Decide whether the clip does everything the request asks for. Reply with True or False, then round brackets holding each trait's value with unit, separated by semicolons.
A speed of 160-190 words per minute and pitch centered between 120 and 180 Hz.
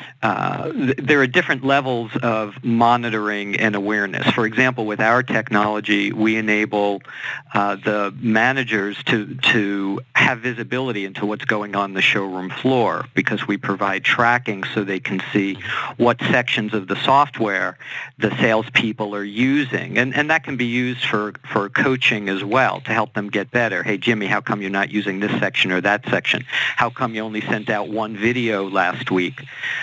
False (175 wpm; 110 Hz)